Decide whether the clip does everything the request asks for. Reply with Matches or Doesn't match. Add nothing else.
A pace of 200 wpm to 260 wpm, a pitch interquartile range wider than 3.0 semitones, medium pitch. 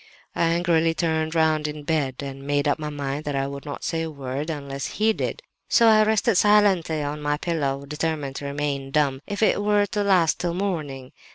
Matches